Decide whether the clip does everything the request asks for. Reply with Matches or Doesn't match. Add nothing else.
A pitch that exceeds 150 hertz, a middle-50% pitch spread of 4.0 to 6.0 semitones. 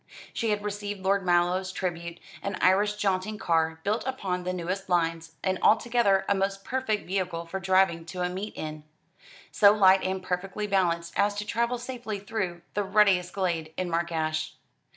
Doesn't match